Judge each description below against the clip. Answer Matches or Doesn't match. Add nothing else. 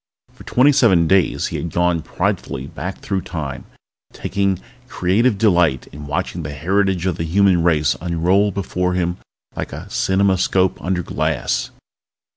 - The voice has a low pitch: Matches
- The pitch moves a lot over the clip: Doesn't match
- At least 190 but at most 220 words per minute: Doesn't match